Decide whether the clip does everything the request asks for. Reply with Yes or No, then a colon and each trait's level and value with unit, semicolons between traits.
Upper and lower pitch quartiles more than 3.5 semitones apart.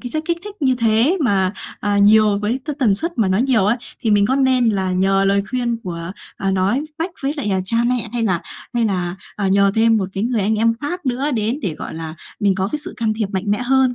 Yes: average, 4.5 semitones